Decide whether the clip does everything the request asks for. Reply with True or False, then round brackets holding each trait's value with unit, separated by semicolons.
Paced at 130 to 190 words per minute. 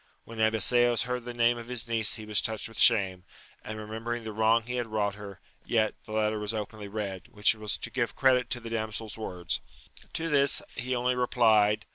False (200 wpm)